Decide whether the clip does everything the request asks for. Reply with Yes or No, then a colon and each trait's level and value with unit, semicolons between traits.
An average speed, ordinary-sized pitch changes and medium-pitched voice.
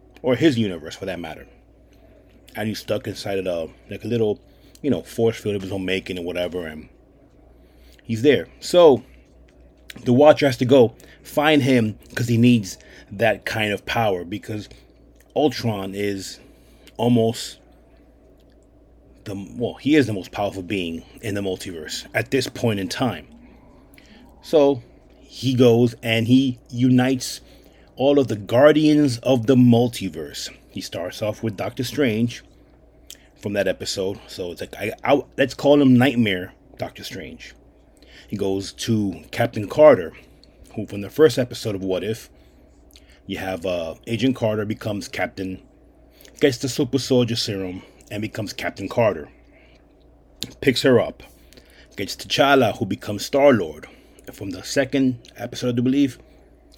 No: average, 150 wpm; average, 4.9 semitones; low, 110 Hz